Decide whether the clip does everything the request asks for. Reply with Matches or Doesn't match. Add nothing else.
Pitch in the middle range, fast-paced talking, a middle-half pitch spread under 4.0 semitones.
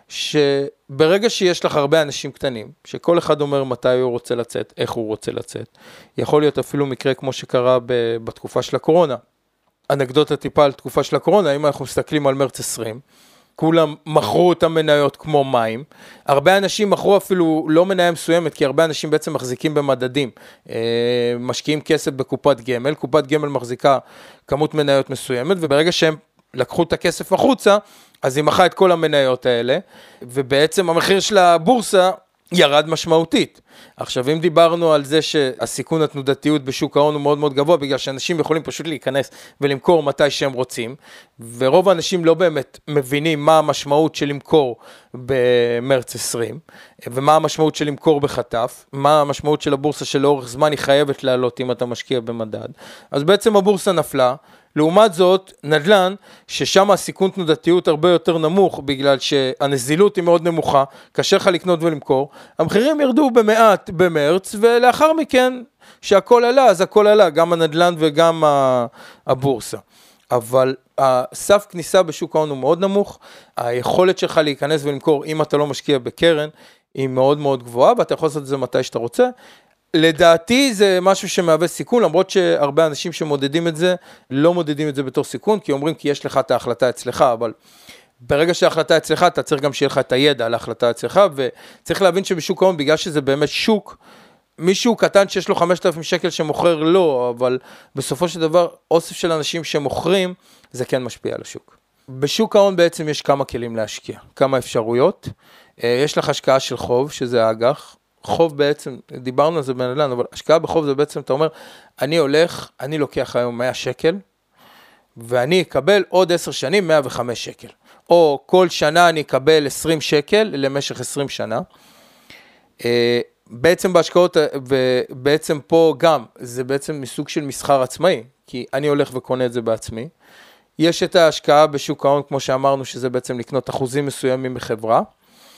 Doesn't match